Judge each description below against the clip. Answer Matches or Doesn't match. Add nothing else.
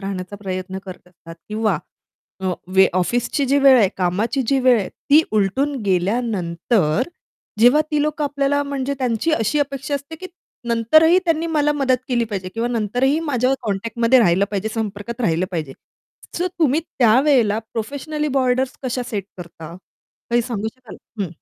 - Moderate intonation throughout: Doesn't match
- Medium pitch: Doesn't match